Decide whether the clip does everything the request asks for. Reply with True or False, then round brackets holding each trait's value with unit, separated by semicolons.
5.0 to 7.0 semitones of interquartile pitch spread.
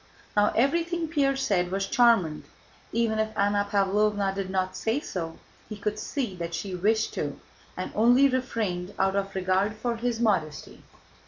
False (3.6 semitones)